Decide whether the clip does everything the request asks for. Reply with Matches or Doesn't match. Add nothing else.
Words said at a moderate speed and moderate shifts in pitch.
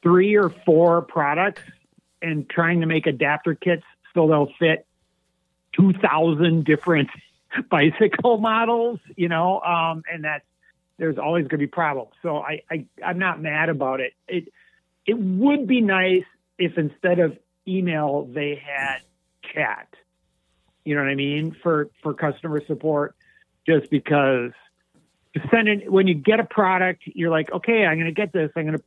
Matches